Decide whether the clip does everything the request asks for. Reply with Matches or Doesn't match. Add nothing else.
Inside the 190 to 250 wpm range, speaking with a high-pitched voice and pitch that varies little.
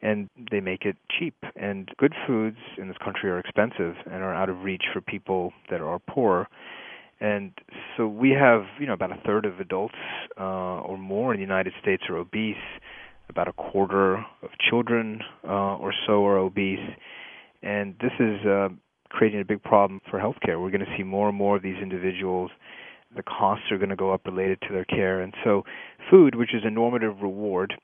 Doesn't match